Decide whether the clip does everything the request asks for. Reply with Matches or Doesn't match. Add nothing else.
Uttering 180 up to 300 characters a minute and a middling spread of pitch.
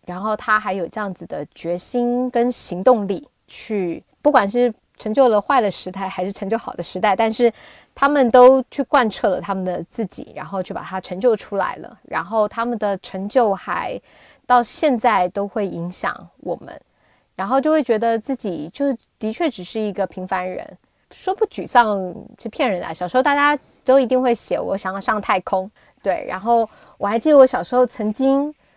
Matches